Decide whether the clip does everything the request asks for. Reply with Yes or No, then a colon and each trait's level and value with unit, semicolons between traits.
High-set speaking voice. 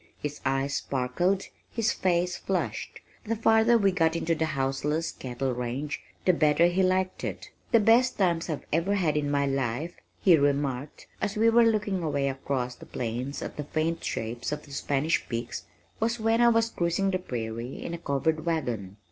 No: medium, 160 Hz